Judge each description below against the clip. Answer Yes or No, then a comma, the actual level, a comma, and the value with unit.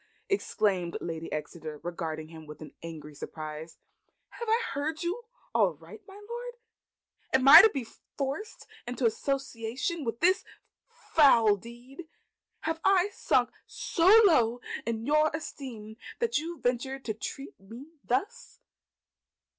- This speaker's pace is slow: Yes, slow, 125 wpm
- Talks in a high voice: Yes, very high, 250 Hz